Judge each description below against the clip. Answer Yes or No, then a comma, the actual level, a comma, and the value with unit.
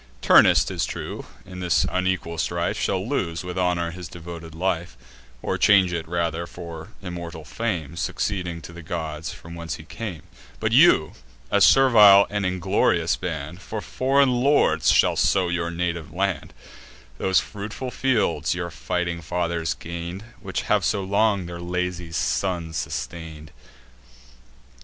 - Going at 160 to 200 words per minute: No, average, 145 wpm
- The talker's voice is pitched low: Yes, very low, 85 Hz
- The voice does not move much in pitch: Yes, narrow, 2.3 semitones